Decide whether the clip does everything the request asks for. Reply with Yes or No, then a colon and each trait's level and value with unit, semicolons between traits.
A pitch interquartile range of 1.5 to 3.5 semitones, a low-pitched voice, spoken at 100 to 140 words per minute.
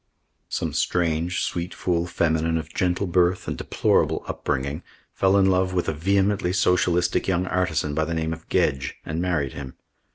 No: narrow, 2.4 semitones; very low, 85 Hz; average, 165 wpm